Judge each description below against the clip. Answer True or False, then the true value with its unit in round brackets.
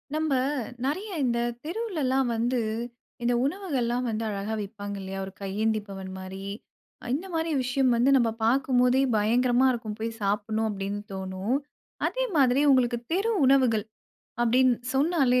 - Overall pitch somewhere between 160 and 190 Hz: False (240 Hz)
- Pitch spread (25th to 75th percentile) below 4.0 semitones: False (4.3 semitones)